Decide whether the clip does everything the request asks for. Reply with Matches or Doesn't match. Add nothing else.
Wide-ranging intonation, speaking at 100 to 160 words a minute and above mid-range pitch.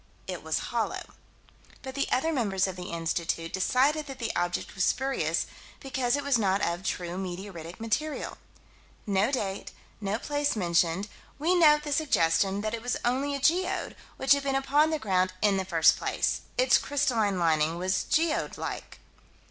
Doesn't match